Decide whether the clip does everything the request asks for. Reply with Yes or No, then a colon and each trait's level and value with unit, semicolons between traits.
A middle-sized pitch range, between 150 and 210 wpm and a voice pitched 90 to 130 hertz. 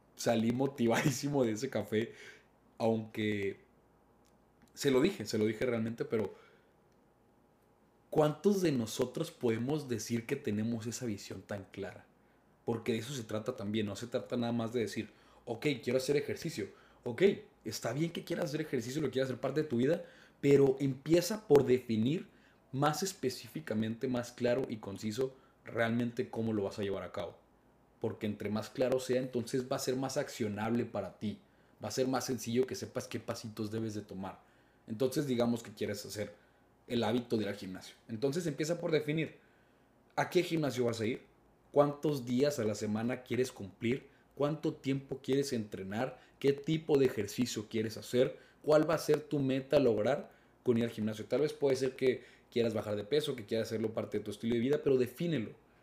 Yes: average, 3.8 semitones; average, 180 wpm; low, 125 Hz